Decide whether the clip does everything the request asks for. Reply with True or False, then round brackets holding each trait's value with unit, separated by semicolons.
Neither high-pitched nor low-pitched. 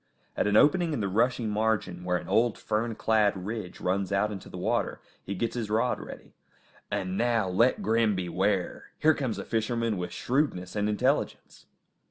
False (105 Hz)